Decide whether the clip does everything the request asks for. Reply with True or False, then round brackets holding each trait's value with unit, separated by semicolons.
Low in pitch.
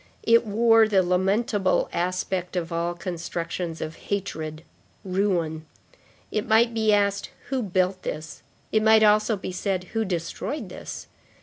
False (190 Hz)